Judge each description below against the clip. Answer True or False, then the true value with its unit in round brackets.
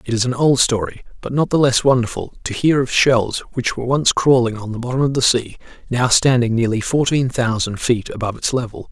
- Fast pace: True (220 wpm)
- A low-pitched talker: True (125 Hz)